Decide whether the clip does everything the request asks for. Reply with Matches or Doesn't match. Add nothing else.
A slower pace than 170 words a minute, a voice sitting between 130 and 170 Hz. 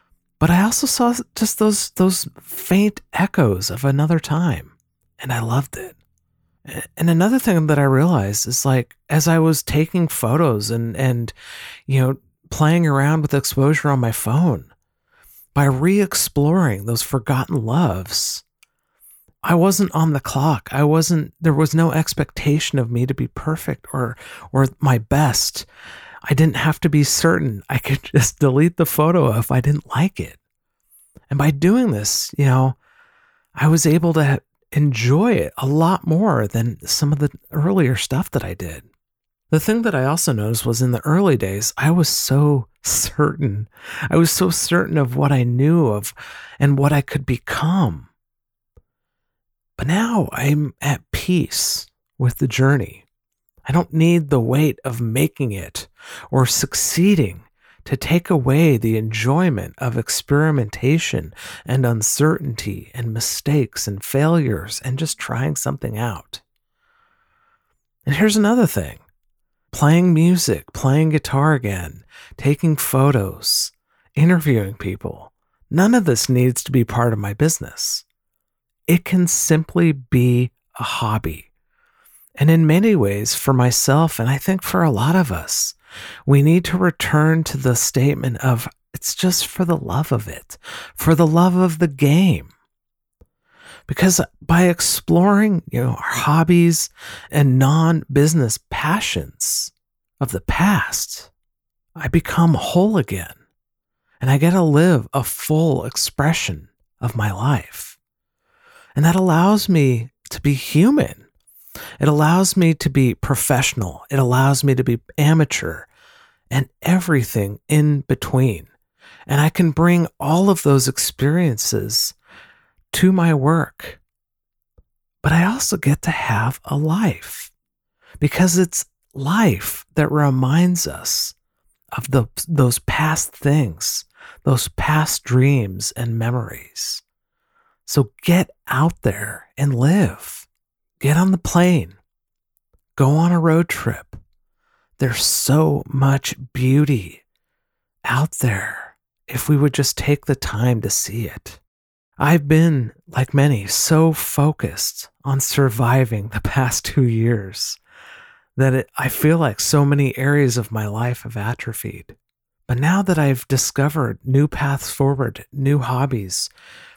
Matches